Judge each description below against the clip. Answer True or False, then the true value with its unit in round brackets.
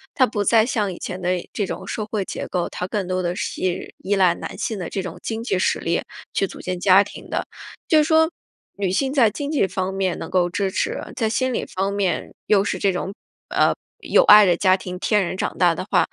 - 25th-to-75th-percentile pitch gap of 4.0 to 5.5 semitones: False (2.9 semitones)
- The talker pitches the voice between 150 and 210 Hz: True (195 Hz)